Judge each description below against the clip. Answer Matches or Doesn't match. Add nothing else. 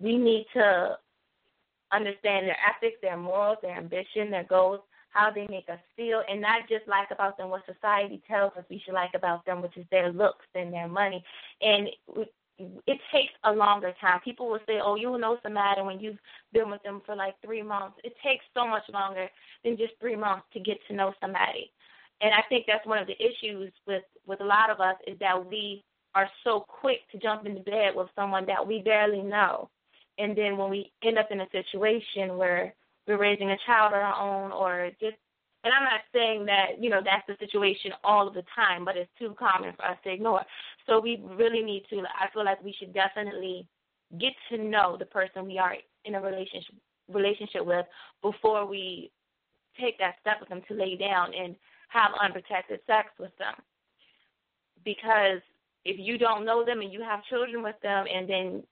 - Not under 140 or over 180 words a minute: Doesn't match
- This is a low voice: Doesn't match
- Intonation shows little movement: Matches